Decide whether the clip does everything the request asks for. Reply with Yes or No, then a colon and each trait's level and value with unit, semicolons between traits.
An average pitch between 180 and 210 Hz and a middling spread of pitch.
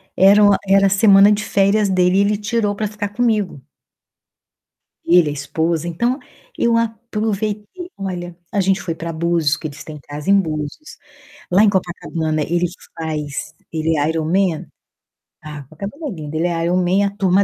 Yes: medium, 185 Hz; average, 4.2 semitones